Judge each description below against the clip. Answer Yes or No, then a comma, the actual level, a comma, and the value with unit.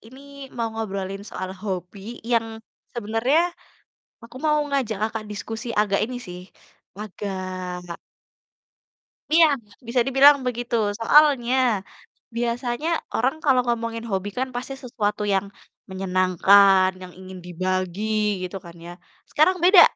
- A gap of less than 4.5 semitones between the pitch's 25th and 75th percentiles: No, average, 4.8 semitones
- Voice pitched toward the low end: No, high, 225 Hz